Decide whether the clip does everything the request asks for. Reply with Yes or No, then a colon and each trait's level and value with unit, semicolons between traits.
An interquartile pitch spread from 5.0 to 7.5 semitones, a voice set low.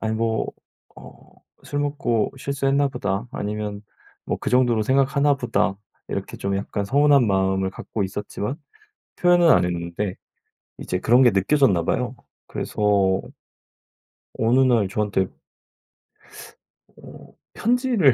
Yes: wide, 5.6 semitones; low, 115 Hz